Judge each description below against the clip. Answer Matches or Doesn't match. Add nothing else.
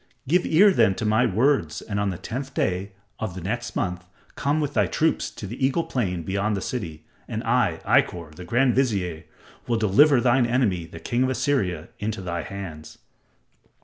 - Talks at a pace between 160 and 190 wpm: Matches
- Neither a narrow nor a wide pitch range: Doesn't match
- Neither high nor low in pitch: Doesn't match